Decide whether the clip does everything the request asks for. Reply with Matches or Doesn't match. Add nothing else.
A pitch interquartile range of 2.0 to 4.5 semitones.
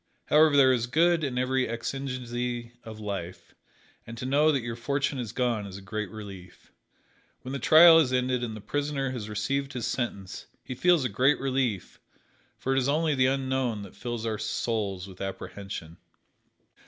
Matches